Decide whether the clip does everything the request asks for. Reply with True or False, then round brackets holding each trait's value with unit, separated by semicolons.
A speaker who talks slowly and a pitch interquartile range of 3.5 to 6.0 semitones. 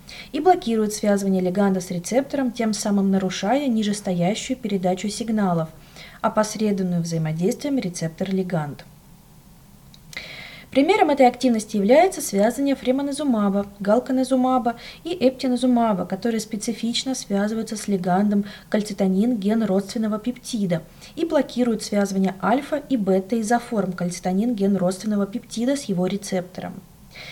True (105 wpm; 4.5 semitones)